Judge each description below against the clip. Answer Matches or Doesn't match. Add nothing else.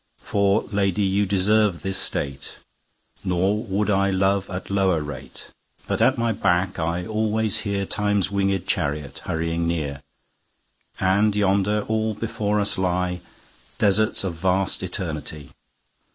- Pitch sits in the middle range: Doesn't match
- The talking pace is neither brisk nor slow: Doesn't match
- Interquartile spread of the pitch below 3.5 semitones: Matches